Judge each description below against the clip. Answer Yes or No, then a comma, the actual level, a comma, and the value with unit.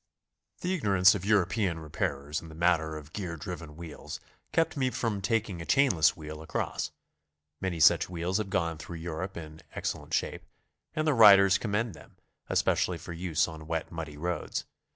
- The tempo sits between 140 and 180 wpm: Yes, average, 170 wpm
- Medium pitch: No, very low, 85 Hz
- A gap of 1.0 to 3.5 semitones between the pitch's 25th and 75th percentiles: No, average, 4.2 semitones